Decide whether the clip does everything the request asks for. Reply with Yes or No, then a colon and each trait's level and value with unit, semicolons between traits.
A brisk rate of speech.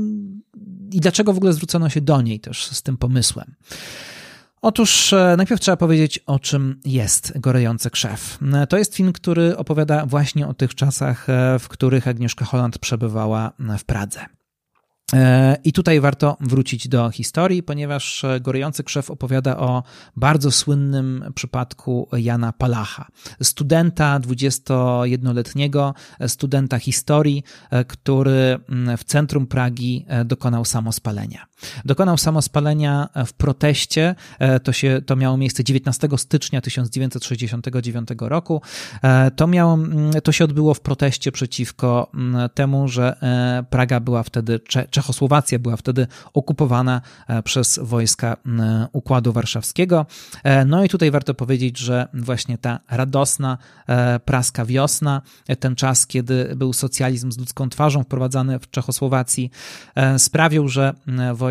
No: average, 120 wpm